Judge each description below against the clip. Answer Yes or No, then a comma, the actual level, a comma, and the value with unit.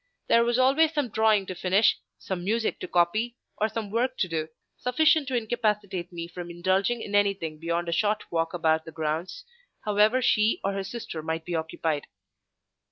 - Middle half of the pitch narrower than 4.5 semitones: No, average, 5.3 semitones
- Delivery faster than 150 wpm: Yes, average, 180 wpm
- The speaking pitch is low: No, high, 200 Hz